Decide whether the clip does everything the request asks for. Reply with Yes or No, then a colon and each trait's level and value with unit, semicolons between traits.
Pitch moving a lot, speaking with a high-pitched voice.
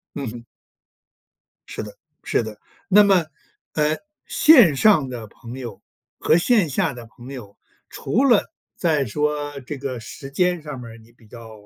No: wide, 5.9 semitones; medium, 140 Hz